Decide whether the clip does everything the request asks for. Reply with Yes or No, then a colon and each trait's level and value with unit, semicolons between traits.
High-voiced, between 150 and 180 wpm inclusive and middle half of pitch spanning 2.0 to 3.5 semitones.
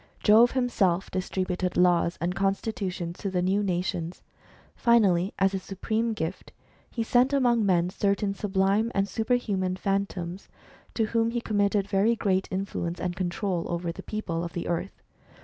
Yes: high, 195 Hz; average, 160 wpm; average, 3.1 semitones